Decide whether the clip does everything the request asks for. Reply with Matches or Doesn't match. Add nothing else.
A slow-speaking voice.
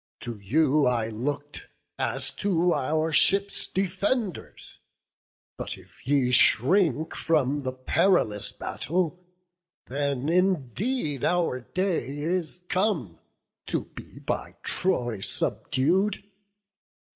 Matches